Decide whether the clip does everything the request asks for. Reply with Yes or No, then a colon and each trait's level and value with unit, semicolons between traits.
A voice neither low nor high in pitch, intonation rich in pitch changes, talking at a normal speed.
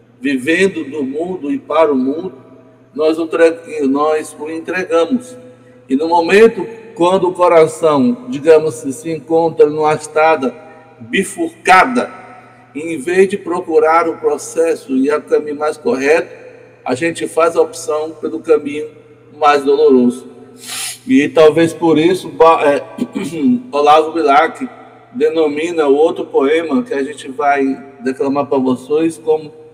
No: medium, 160 Hz; average, 3.6 semitones; average, 130 wpm